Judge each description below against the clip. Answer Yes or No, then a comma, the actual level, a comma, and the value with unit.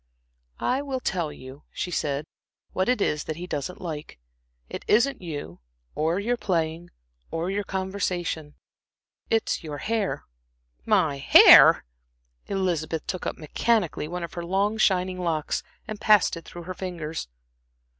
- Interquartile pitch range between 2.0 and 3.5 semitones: No, average, 4.0 semitones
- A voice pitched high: No, medium, 175 Hz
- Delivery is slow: No, average, 145 wpm